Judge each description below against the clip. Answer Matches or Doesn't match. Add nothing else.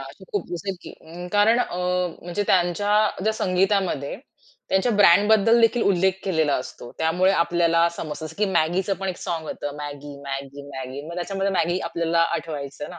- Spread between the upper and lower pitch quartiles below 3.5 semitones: Doesn't match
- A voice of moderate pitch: Matches